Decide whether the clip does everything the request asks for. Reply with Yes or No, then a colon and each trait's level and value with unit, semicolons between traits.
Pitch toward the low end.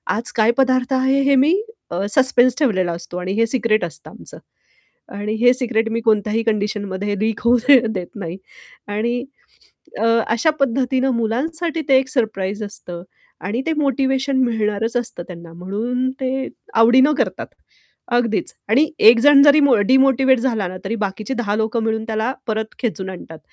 No: high, 230 Hz